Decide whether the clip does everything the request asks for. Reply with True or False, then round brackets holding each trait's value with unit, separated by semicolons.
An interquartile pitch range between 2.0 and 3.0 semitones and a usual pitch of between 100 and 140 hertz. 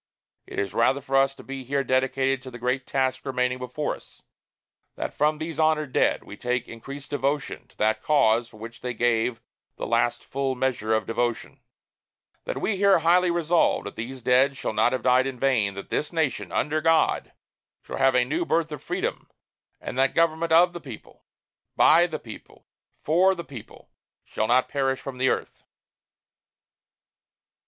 False (3.8 semitones; 135 Hz)